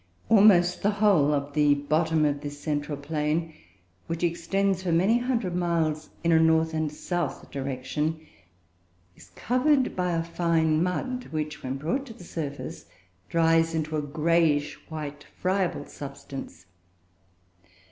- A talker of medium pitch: Yes, medium, 160 Hz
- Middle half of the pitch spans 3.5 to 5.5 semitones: No, average, 3.1 semitones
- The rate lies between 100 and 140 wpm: Yes, slow, 135 wpm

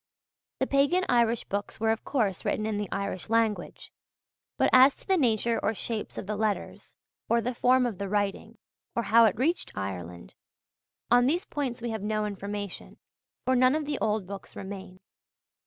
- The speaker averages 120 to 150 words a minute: No, average, 180 wpm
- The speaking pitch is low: No, high, 220 Hz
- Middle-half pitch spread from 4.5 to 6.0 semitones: No, average, 3.7 semitones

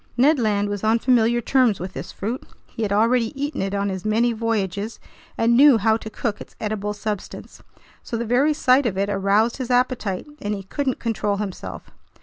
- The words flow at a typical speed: Yes, average, 195 wpm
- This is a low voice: No, high, 220 Hz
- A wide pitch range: No, average, 3.2 semitones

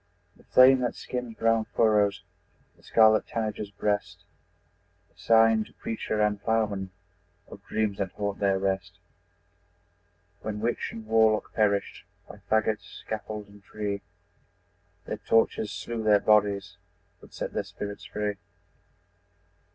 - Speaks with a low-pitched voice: Yes, low, 105 Hz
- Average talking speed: No, slow, 130 wpm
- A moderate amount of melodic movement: No, narrow, 1.6 semitones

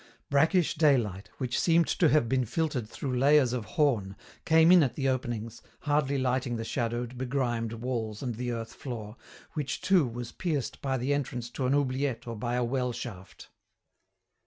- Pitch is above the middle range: No, low, 125 Hz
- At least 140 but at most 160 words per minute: No, average, 175 wpm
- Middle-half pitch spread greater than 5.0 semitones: No, average, 3.4 semitones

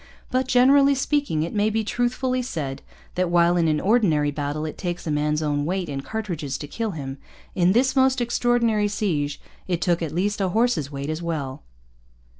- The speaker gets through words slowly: No, average, 190 wpm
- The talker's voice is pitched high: No, medium, 175 Hz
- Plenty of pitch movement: Yes, wide, 7.6 semitones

